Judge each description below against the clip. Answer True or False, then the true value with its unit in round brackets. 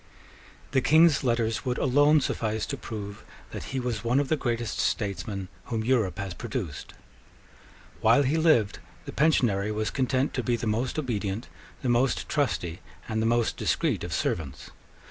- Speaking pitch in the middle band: False (120 Hz)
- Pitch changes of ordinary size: True (3.8 semitones)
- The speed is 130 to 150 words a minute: False (165 wpm)